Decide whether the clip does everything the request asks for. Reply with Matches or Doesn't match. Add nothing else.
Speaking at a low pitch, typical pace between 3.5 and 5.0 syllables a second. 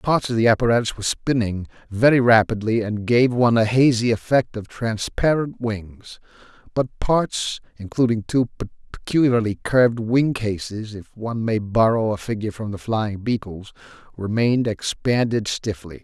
Matches